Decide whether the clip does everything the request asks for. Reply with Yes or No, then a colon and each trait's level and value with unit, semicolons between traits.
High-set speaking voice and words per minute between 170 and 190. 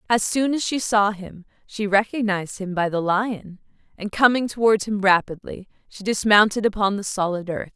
Yes: high, 205 Hz; average, 180 wpm